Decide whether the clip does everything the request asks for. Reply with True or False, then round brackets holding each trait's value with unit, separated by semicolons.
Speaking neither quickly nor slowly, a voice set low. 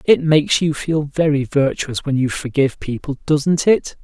False (180 wpm; 145 Hz)